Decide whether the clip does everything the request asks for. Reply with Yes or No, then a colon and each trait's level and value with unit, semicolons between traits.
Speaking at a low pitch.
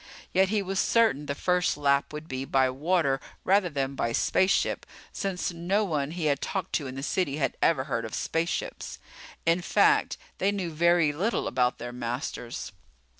No: medium, 155 Hz